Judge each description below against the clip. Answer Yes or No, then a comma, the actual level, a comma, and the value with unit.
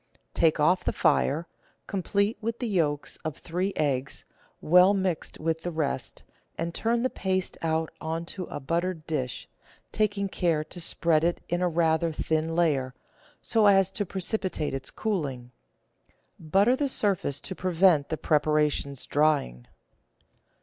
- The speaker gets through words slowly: No, average, 150 wpm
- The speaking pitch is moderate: Yes, medium, 165 Hz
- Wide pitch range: No, average, 3.8 semitones